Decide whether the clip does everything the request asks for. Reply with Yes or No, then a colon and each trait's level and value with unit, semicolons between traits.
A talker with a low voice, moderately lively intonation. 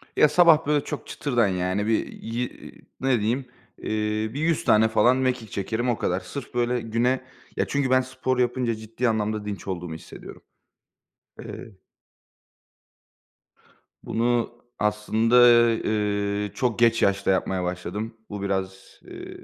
Yes: low, 115 Hz; average, 3.7 semitones